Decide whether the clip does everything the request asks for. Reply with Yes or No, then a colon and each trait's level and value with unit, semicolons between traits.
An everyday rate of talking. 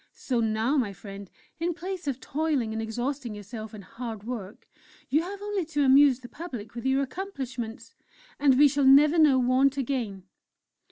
Yes: average, 170 wpm